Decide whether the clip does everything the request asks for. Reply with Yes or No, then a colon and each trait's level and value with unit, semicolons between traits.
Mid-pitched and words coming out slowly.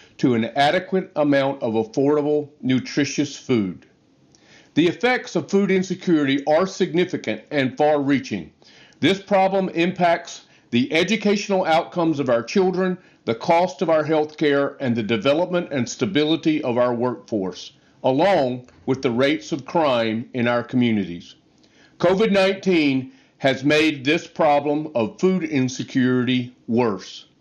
Yes: medium, 150 Hz; slow, 130 wpm